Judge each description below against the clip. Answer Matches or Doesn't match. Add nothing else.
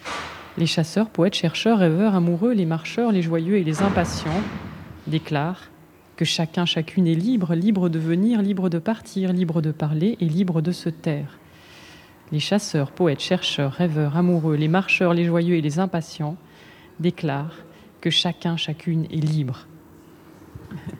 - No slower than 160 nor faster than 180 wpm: Doesn't match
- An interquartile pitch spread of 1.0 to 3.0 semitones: Matches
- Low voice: Doesn't match